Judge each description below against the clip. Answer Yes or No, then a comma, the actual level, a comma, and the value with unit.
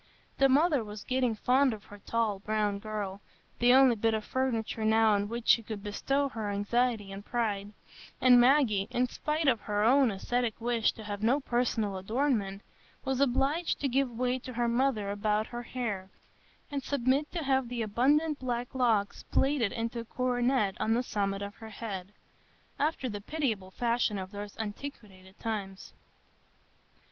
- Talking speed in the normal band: Yes, average, 165 wpm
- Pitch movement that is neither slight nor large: Yes, average, 3.8 semitones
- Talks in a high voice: Yes, high, 230 Hz